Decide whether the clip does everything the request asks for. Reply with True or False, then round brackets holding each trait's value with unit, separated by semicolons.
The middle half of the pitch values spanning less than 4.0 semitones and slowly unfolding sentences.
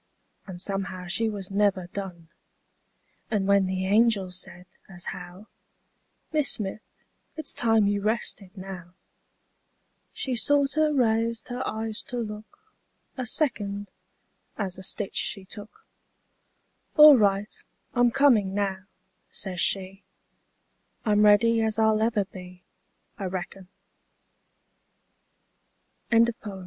True (3.1 semitones; 120 wpm)